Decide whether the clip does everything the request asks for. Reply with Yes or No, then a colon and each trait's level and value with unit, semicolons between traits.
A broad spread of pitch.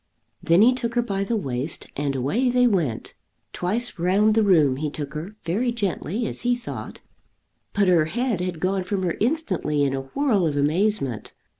Yes: wide, 7.0 semitones